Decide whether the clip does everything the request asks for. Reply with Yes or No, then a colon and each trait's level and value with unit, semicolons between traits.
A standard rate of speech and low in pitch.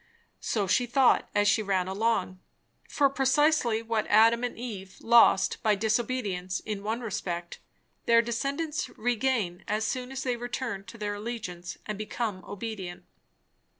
No: average, 145 wpm; high, 220 Hz